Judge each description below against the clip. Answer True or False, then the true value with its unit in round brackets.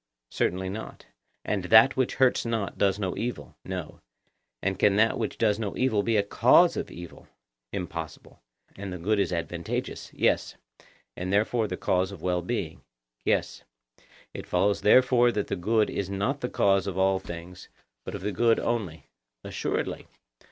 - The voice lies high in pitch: False (100 Hz)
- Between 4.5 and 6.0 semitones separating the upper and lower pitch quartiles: False (3.4 semitones)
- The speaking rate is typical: True (165 wpm)